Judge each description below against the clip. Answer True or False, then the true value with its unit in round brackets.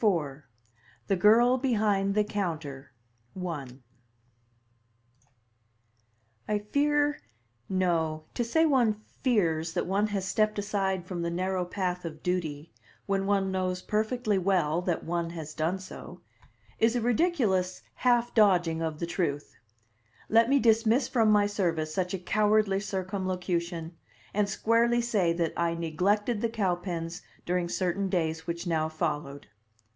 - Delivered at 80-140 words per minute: True (135 wpm)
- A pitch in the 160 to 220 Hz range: True (190 Hz)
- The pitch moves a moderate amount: True (3.9 semitones)